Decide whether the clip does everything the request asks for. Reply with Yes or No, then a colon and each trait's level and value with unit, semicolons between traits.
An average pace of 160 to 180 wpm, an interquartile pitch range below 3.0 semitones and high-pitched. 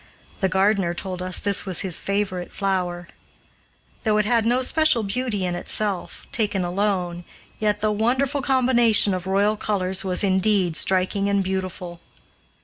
No: average, 145 wpm; narrow, 2.6 semitones; high, 195 Hz